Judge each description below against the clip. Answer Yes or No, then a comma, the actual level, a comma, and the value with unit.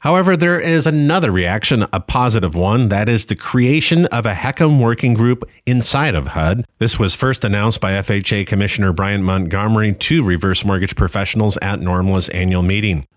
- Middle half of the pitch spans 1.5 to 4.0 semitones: No, average, 4.5 semitones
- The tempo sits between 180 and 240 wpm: No, average, 170 wpm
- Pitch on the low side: Yes, low, 105 Hz